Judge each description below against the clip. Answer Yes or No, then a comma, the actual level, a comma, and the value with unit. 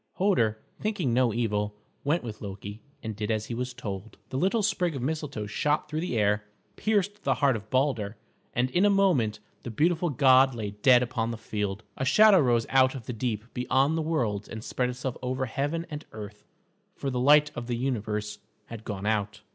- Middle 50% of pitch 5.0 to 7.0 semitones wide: Yes, wide, 5.5 semitones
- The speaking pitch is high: No, low, 125 Hz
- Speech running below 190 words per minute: No, average, 200 wpm